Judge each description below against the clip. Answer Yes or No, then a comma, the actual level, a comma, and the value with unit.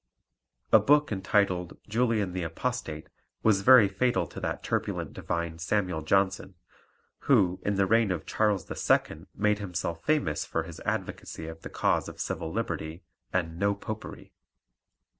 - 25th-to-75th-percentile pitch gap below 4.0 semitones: No, average, 4.3 semitones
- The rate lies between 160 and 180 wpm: No, average, 145 wpm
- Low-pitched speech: Yes, very low, 95 Hz